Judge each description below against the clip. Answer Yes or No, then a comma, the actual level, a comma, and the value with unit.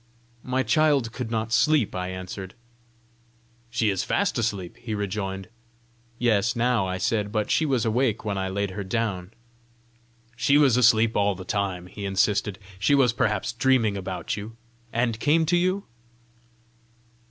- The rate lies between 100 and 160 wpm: Yes, average, 155 wpm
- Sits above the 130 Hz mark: No, low, 110 Hz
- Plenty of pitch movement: No, average, 4.0 semitones